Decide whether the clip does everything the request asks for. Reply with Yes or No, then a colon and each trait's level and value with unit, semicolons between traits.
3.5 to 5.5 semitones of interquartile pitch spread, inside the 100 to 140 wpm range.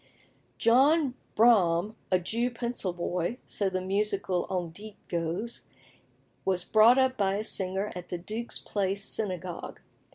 Yes: average, 4.1 semitones; slow, 135 wpm